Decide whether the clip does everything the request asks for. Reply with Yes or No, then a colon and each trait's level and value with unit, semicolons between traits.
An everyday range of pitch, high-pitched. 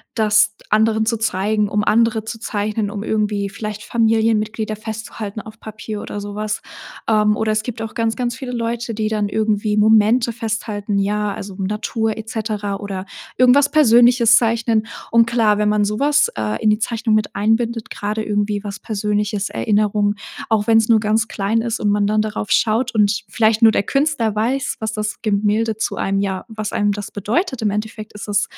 No: narrow, 1.5 semitones; high, 215 Hz